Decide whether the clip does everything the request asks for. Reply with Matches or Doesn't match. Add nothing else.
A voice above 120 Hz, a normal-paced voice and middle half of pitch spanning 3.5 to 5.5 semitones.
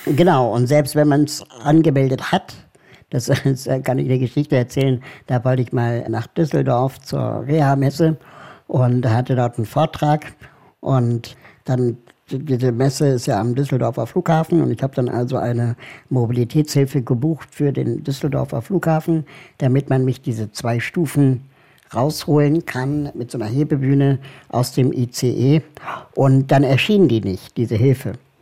Doesn't match